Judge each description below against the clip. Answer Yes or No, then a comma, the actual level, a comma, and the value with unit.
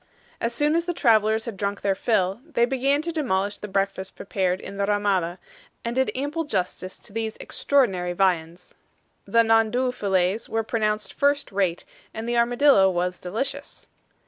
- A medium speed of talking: Yes, average, 165 wpm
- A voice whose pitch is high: Yes, high, 215 Hz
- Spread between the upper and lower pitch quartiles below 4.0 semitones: No, average, 4.9 semitones